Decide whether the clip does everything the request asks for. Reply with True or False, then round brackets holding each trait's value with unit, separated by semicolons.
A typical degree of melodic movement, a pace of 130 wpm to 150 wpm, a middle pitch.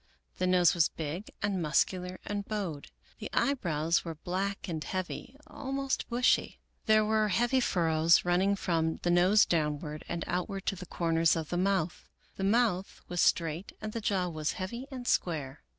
False (3.9 semitones; 165 wpm; 180 Hz)